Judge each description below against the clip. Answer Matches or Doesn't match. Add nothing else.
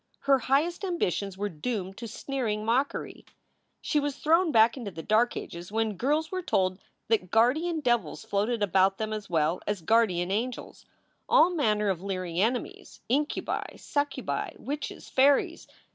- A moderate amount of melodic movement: Doesn't match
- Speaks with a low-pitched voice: Doesn't match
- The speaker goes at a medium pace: Matches